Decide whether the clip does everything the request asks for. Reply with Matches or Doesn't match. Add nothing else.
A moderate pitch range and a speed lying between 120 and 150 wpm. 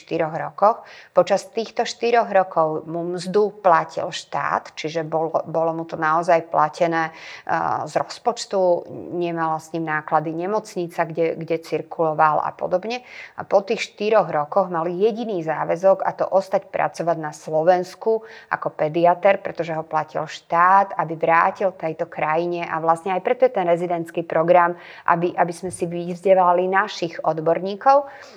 Matches